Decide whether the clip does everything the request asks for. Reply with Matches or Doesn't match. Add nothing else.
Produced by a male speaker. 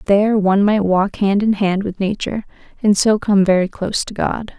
Doesn't match